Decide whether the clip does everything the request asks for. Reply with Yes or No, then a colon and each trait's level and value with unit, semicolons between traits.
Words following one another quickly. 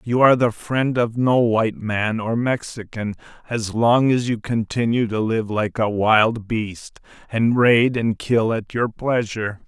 No: average, 175 wpm